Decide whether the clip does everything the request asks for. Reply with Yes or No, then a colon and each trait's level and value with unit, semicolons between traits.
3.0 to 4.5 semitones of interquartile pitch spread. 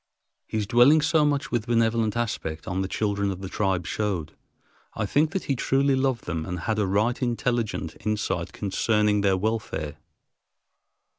Yes: average, 3.9 semitones